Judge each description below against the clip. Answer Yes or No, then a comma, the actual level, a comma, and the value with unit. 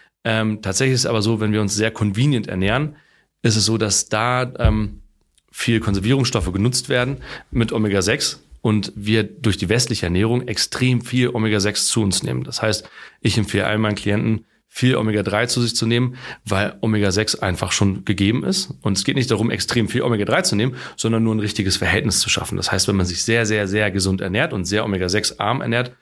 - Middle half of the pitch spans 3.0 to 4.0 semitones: No, narrow, 2.5 semitones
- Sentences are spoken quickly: Yes, fast, 200 wpm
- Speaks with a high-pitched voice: No, low, 110 Hz